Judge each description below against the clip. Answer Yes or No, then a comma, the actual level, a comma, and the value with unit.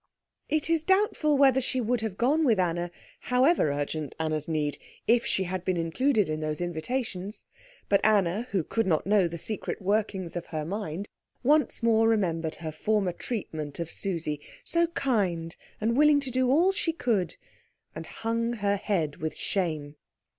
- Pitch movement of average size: No, wide, 6.9 semitones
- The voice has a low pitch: No, high, 200 Hz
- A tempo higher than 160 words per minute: Yes, average, 170 wpm